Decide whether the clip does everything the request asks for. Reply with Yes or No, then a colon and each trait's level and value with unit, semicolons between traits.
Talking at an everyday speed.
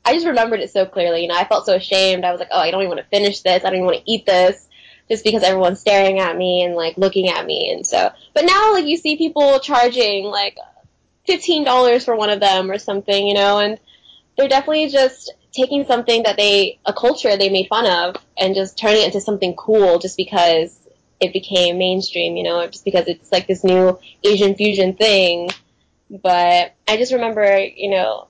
No: fast, 220 wpm